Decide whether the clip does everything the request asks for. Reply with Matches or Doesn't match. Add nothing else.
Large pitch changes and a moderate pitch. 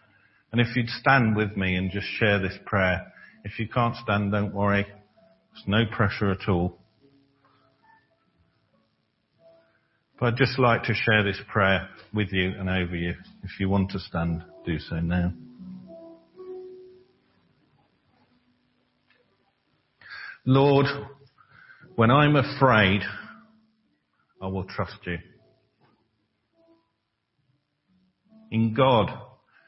Doesn't match